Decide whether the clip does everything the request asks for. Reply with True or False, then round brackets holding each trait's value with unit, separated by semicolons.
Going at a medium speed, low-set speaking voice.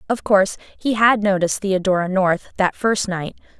False (165 wpm; 195 Hz)